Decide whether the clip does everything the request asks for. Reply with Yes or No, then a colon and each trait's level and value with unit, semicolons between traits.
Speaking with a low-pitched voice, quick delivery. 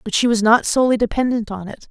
No: high, 230 Hz; fast, 250 wpm